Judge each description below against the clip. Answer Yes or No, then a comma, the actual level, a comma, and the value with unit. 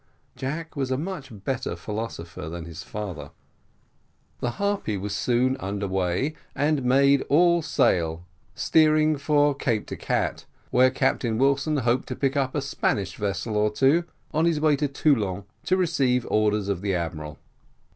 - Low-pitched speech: Yes, low, 130 Hz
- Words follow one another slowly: No, average, 160 wpm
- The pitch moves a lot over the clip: Yes, wide, 6.4 semitones